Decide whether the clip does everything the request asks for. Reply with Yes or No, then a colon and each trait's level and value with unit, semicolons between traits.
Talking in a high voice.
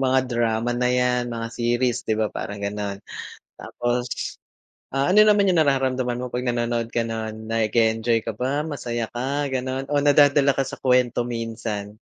No: low, 120 Hz